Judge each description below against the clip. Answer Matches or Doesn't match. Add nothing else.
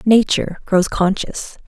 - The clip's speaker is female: Matches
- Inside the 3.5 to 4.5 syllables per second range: Matches